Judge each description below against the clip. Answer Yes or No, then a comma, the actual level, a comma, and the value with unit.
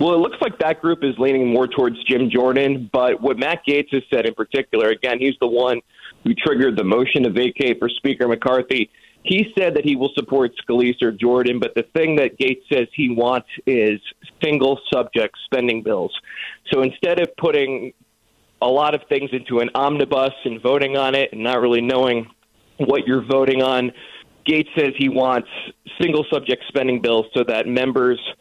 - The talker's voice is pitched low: Yes, low, 130 Hz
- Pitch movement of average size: No, narrow, 2.2 semitones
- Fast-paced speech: No, average, 190 wpm